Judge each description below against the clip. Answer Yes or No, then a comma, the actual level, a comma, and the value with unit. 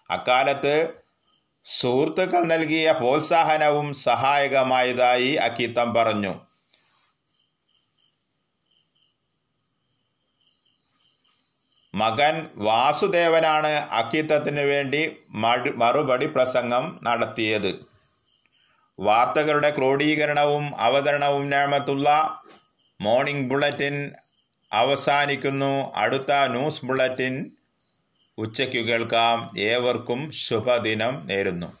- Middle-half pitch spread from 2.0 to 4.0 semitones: Yes, average, 3.2 semitones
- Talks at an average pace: No, slow, 55 wpm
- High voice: No, medium, 140 Hz